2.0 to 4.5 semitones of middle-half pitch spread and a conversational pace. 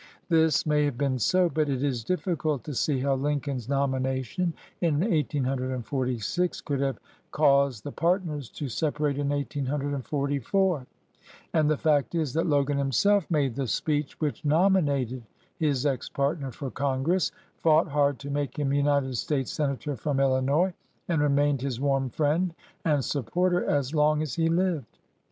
Yes: narrow, 2.5 semitones; average, 155 wpm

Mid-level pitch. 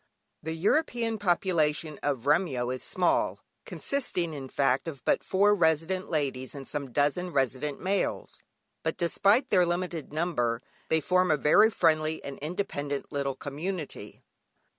Yes: medium, 160 Hz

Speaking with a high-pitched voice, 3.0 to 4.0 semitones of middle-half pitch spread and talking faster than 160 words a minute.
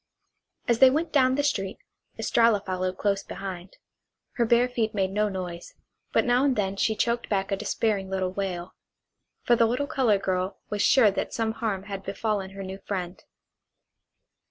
Yes: high, 205 Hz; average, 3.5 semitones; average, 175 wpm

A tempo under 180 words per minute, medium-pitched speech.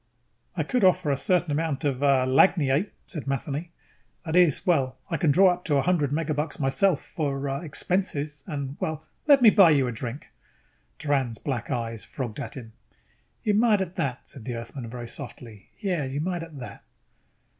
No: average, 185 wpm; medium, 145 Hz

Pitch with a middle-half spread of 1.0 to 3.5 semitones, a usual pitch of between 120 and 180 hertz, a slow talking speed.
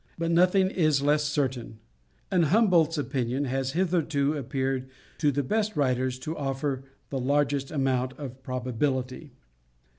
Yes: average, 3.1 semitones; medium, 140 Hz; slow, 130 wpm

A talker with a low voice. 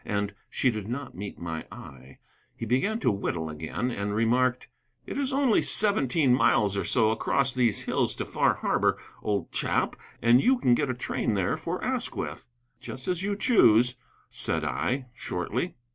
Yes: low, 120 Hz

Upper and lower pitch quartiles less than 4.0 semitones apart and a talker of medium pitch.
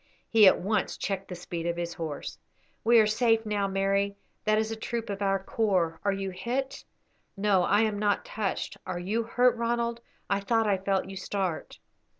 No: average, 2.7 semitones; high, 200 Hz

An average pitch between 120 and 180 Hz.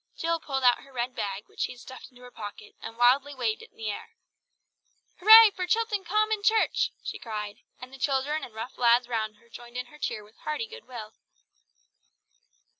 No: very high, 255 Hz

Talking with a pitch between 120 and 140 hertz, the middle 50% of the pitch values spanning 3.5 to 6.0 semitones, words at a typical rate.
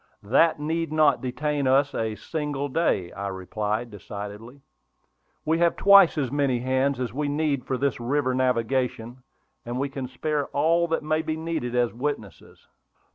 Yes: low, 135 Hz; average, 4.0 semitones; average, 160 wpm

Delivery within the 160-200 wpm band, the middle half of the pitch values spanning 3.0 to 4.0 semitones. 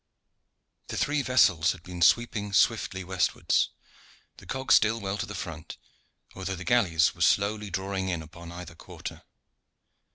No: average, 150 wpm; average, 3.3 semitones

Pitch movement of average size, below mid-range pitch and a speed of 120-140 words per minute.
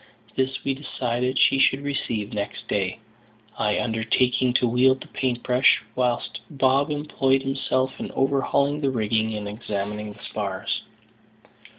Yes: average, 3.6 semitones; low, 125 Hz; slow, 135 wpm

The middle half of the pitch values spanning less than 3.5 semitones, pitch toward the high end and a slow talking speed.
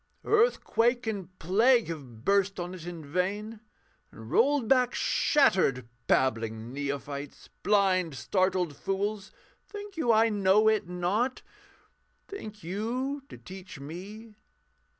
No: wide, 5.4 semitones; high, 195 Hz; slow, 115 wpm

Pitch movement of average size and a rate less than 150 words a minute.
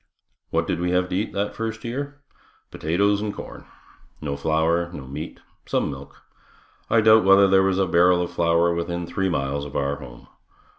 No: average, 4.1 semitones; average, 185 wpm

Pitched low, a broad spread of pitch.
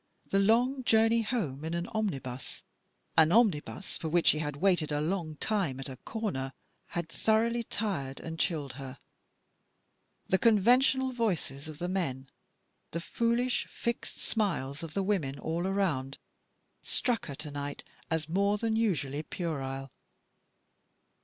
No: medium, 170 Hz; wide, 7.2 semitones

